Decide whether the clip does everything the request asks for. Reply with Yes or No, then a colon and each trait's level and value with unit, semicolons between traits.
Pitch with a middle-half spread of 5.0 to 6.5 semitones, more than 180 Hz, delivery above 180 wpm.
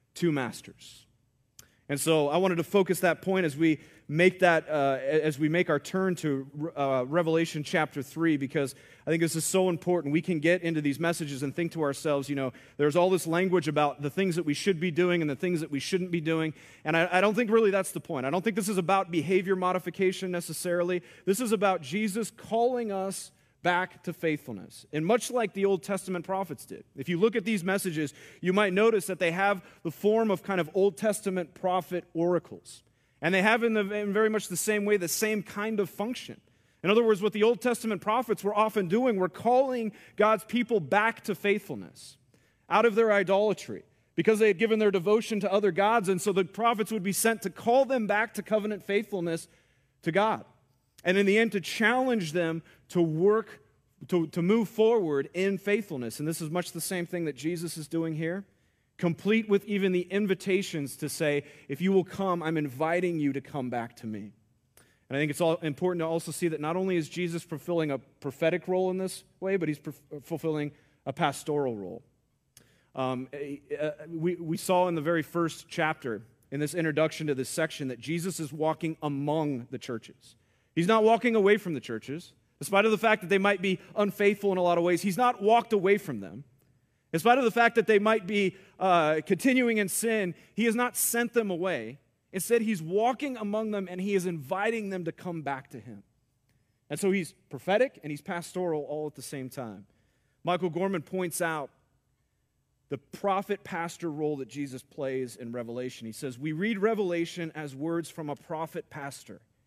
No: average, 5.3 semitones; medium, 175 Hz; fast, 205 wpm